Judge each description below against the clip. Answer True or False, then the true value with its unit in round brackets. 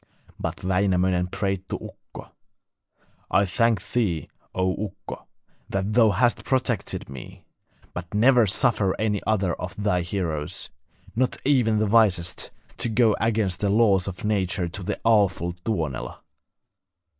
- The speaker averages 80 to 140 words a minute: True (135 wpm)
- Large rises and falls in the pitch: False (3.3 semitones)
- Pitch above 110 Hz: False (100 Hz)